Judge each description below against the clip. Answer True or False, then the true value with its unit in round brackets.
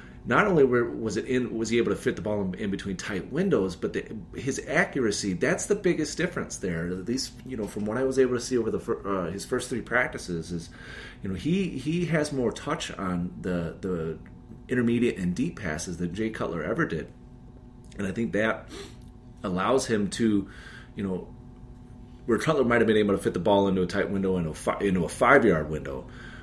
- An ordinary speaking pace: False (210 wpm)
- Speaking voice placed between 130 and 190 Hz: False (110 Hz)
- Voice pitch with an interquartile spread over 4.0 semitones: True (5.2 semitones)